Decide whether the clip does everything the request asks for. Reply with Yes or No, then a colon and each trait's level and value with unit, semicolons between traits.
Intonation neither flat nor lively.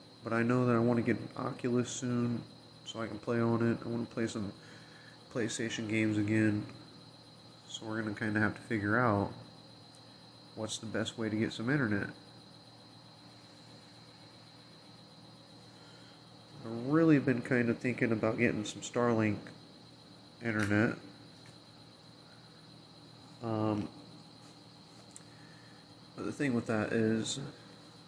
Yes: average, 3.1 semitones